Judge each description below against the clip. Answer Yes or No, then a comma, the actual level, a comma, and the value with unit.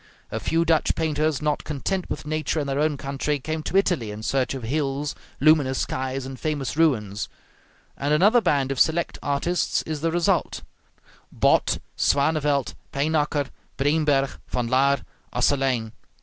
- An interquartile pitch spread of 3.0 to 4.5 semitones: No, narrow, 2.5 semitones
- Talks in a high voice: No, medium, 145 Hz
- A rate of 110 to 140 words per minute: No, average, 150 wpm